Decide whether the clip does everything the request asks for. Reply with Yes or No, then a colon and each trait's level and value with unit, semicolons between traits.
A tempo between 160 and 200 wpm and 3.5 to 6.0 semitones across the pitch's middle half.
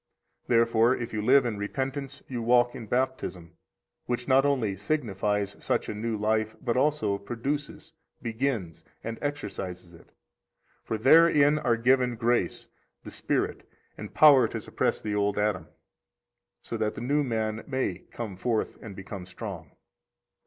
No: average, 150 wpm; average, 4.1 semitones